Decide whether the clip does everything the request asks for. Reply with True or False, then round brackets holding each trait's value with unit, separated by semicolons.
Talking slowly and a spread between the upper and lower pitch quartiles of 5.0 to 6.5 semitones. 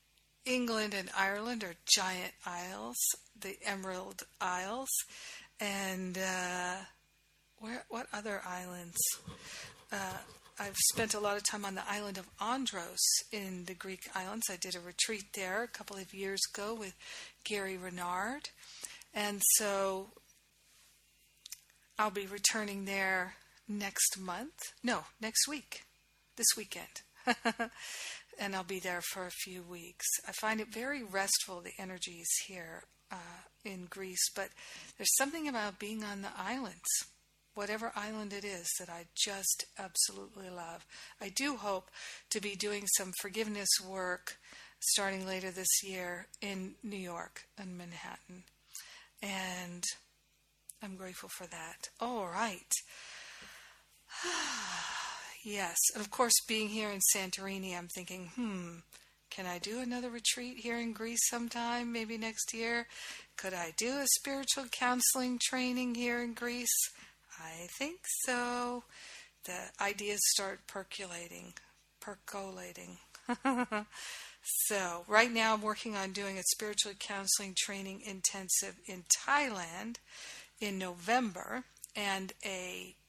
False (130 wpm; 3.3 semitones)